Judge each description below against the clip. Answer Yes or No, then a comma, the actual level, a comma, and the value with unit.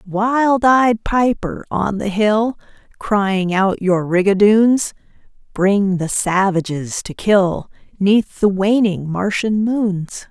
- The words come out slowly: Yes, slow, 115 wpm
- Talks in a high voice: Yes, high, 205 Hz